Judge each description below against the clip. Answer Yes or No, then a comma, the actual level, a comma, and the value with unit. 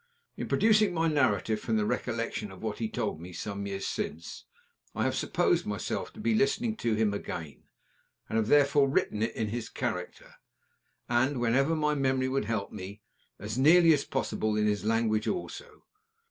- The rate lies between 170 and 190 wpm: Yes, average, 175 wpm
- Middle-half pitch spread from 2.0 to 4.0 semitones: No, wide, 5.4 semitones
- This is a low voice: Yes, low, 115 Hz